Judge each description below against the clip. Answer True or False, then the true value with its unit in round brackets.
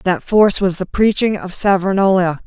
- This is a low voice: False (190 Hz)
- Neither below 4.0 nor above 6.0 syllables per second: True (5.4 syllables/s)